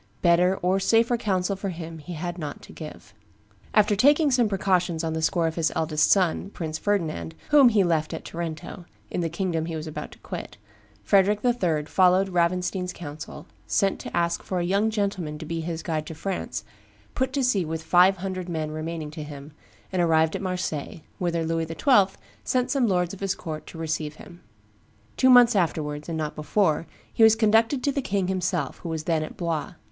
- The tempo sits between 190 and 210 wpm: Yes, average, 200 wpm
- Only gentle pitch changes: No, average, 3.6 semitones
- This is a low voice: No, medium, 175 Hz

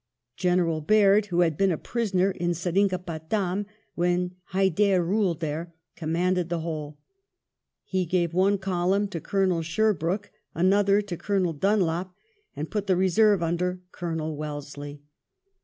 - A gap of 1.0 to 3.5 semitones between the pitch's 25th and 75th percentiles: Yes, average, 2.8 semitones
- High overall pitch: No, medium, 180 Hz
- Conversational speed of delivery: No, slow, 130 wpm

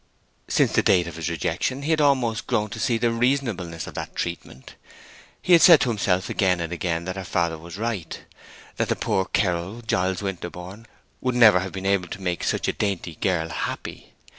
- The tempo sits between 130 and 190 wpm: No, average, 200 wpm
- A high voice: No, very low, 95 Hz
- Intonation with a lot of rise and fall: No, average, 4.8 semitones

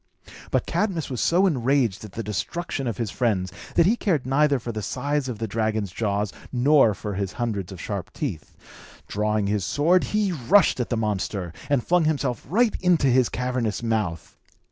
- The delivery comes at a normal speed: Yes, average, 185 wpm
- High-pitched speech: No, low, 120 Hz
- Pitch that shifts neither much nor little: No, wide, 5.9 semitones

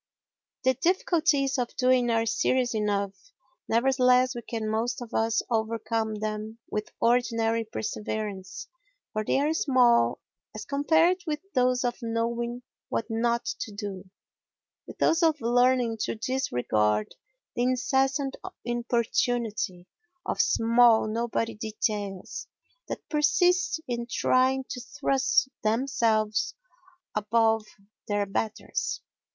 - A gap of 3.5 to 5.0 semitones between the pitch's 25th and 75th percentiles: No, average, 3.0 semitones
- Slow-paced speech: Yes, slow, 110 wpm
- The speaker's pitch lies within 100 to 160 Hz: No, high, 235 Hz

